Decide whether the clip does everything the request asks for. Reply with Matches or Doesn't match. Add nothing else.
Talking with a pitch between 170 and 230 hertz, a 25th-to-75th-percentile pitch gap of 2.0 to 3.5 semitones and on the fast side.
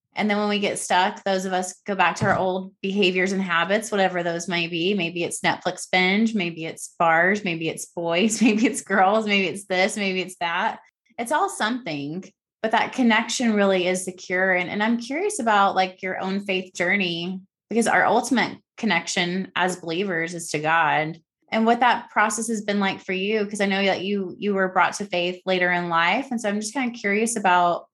Matches